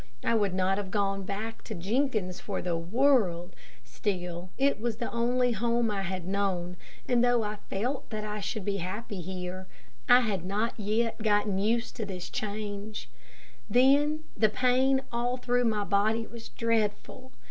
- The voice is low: No, high, 210 Hz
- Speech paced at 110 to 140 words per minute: No, average, 165 wpm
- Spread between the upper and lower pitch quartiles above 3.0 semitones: Yes, average, 3.6 semitones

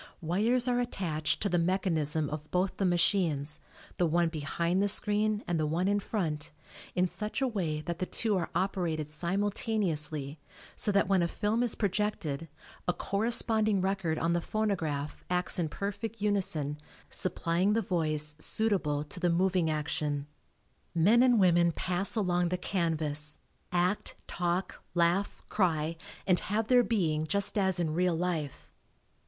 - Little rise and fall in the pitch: No, average, 4.1 semitones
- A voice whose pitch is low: No, medium, 180 Hz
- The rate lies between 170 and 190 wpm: No, average, 155 wpm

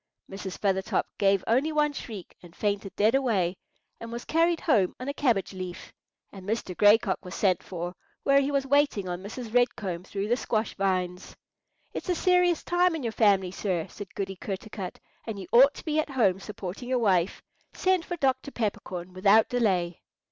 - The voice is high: Yes, high, 210 Hz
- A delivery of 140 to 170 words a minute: No, average, 190 wpm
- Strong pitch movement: Yes, wide, 5.9 semitones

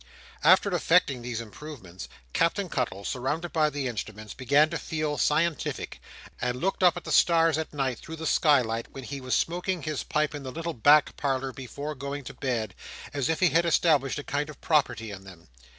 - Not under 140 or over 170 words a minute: No, average, 195 wpm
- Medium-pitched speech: Yes, medium, 145 Hz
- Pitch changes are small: No, average, 4.3 semitones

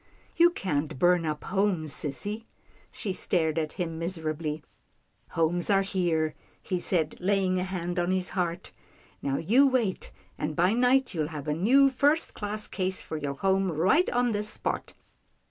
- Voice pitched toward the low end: No, medium, 180 Hz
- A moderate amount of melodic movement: Yes, average, 4.3 semitones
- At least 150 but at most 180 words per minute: Yes, average, 175 wpm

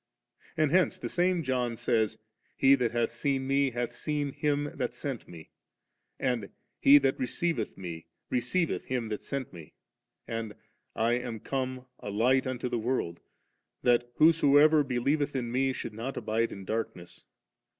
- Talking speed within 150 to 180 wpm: Yes, average, 160 wpm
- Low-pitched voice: Yes, low, 125 Hz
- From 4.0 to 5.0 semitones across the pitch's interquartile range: No, average, 3.5 semitones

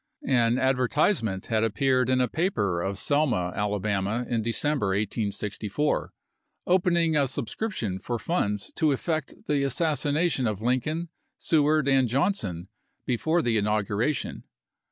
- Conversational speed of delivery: No, slow, 125 wpm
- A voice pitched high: No, low, 125 Hz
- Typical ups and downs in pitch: No, wide, 6.2 semitones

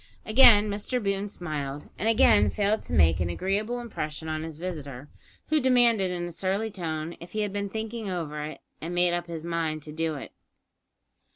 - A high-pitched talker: No, medium, 175 Hz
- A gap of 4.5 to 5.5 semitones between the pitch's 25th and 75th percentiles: Yes, average, 5.2 semitones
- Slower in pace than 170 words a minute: No, average, 190 wpm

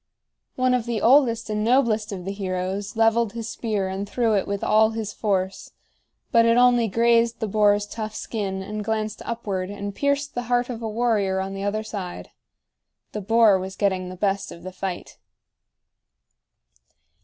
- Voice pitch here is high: Yes, high, 215 Hz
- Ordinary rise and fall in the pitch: Yes, average, 3.0 semitones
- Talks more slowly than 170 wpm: No, average, 175 wpm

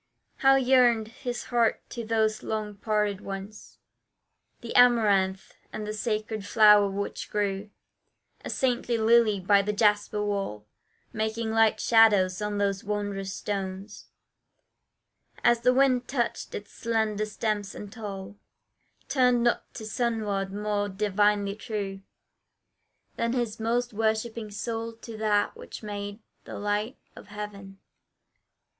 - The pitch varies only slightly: Yes, narrow, 2.1 semitones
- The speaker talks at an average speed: No, slow, 125 wpm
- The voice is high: Yes, high, 215 Hz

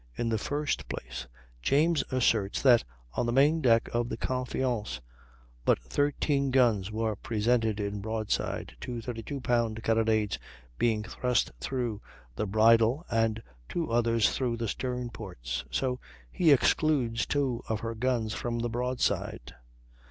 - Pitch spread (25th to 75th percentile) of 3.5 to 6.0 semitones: No, average, 2.7 semitones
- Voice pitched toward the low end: Yes, low, 115 Hz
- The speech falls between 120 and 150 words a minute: Yes, average, 140 wpm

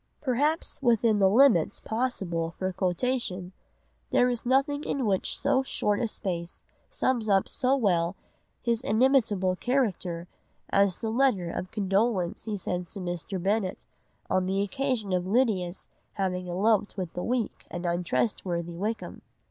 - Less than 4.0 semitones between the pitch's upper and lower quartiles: No, average, 5.0 semitones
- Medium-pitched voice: No, high, 200 Hz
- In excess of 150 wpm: No, average, 140 wpm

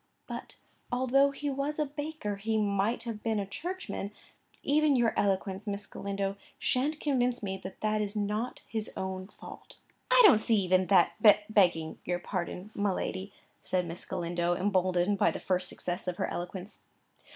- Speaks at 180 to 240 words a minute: No, average, 165 wpm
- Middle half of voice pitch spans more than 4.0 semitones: Yes, average, 4.6 semitones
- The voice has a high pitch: Yes, high, 205 Hz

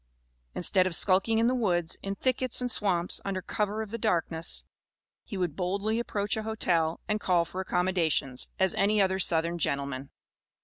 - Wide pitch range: No, average, 3.8 semitones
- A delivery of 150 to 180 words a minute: Yes, average, 170 wpm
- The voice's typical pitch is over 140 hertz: Yes, high, 190 Hz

